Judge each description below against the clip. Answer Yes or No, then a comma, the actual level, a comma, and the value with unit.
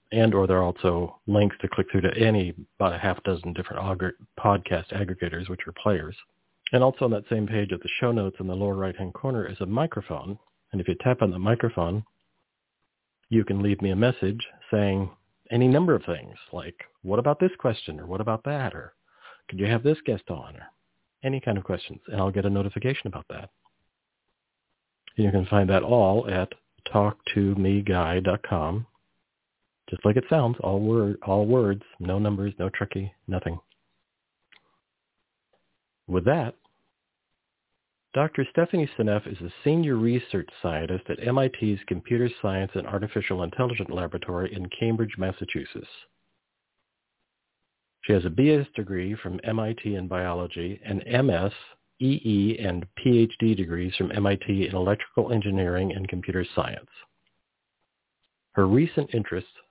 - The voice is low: Yes, low, 100 Hz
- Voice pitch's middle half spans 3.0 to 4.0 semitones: Yes, average, 3.6 semitones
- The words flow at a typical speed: Yes, average, 155 wpm